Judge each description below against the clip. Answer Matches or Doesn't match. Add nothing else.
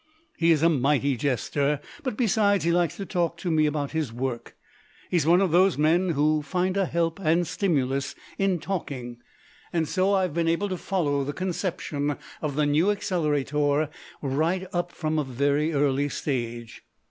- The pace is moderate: Matches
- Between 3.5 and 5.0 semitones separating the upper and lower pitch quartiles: Matches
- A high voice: Doesn't match